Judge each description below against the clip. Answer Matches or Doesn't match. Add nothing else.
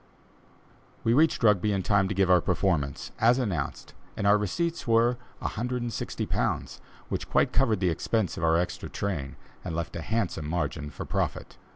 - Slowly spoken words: Doesn't match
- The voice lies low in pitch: Matches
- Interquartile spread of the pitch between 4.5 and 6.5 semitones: Matches